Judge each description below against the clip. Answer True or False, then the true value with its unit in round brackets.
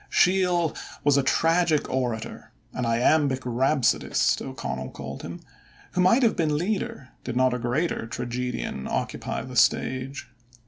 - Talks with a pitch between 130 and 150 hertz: True (135 Hz)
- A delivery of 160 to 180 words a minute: False (135 wpm)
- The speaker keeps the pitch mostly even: False (5.0 semitones)